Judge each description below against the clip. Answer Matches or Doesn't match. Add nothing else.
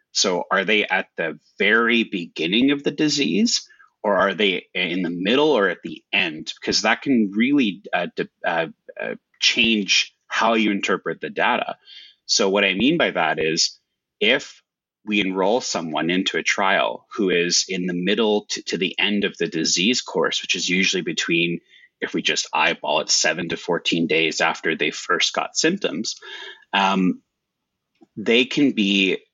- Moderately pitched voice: Doesn't match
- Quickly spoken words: Doesn't match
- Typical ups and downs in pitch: Doesn't match